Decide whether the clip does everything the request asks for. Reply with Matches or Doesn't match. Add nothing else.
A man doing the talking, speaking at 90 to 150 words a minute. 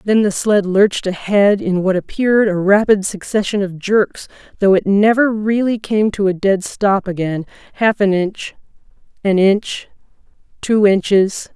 Doesn't match